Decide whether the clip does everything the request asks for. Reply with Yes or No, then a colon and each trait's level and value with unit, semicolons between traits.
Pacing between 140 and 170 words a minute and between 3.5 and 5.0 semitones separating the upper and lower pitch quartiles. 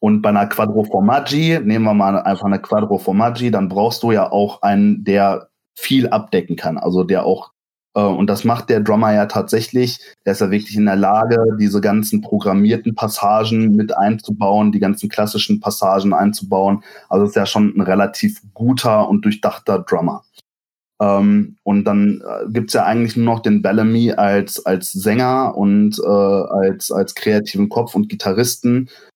No: average, 165 wpm; narrow, 2.5 semitones